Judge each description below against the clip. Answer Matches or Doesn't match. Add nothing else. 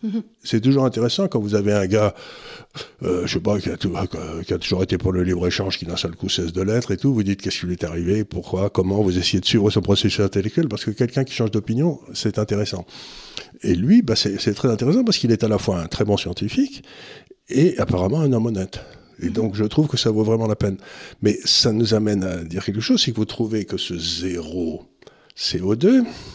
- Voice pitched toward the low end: Matches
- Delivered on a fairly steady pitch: Doesn't match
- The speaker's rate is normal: Doesn't match